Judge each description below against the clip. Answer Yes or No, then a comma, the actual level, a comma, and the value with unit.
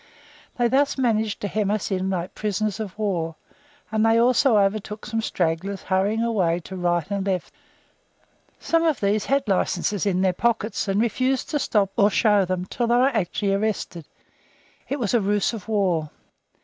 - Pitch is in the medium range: No, high, 205 Hz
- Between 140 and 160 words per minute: No, average, 175 wpm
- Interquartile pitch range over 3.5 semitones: No, average, 3.2 semitones